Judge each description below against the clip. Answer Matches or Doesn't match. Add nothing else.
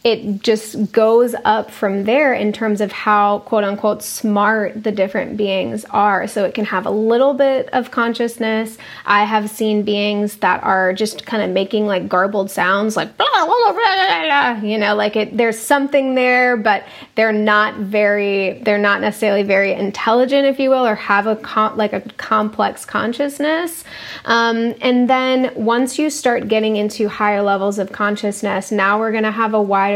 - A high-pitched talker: Matches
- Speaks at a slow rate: Doesn't match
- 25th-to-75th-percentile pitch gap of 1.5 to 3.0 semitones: Matches